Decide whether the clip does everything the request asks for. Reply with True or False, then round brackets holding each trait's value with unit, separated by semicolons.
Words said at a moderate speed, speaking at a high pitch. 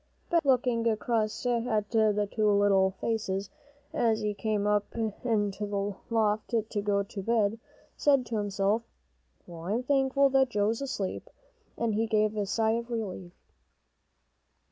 True (145 wpm; 215 Hz)